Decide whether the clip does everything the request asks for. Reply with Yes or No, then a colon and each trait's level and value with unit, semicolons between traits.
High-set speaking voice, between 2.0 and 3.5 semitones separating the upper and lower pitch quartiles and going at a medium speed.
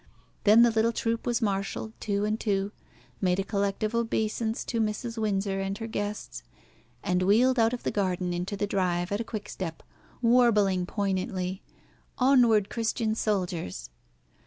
Yes: high, 205 Hz; average, 2.8 semitones; average, 155 wpm